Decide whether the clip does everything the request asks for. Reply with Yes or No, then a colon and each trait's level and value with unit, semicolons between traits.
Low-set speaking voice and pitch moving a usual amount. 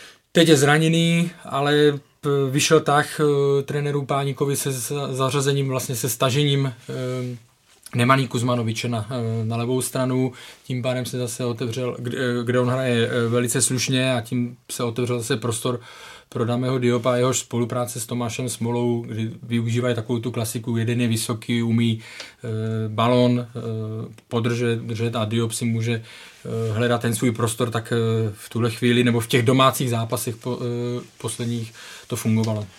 No: low, 125 Hz; narrow, 2.0 semitones